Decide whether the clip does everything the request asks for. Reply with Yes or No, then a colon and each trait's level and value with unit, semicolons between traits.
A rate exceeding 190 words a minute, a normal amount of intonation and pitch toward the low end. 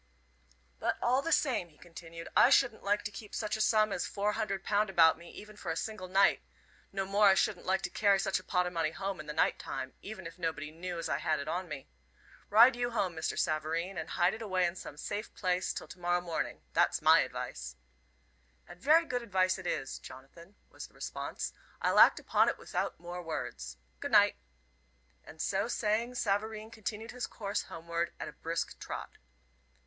No: fast, 205 wpm; average, 4.1 semitones; high, 190 Hz